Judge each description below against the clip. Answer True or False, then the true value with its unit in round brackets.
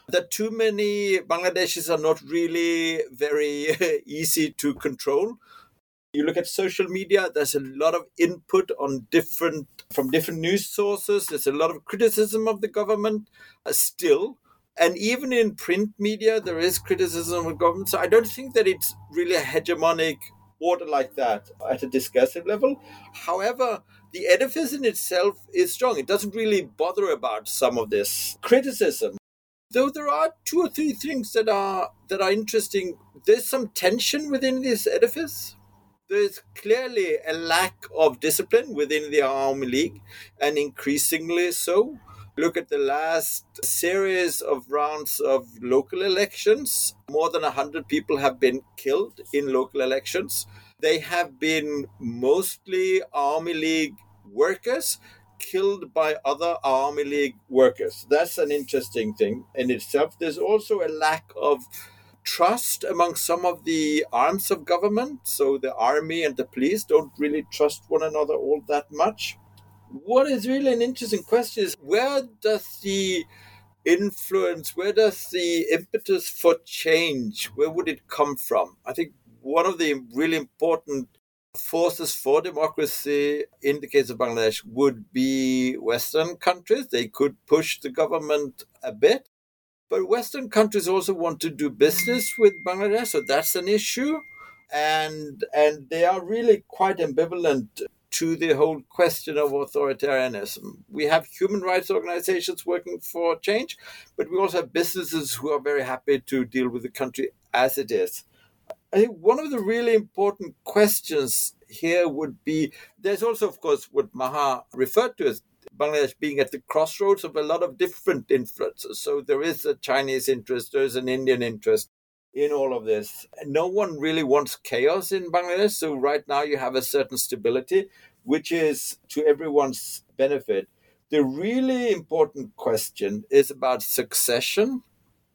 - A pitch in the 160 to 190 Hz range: True (185 Hz)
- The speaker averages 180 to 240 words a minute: False (155 wpm)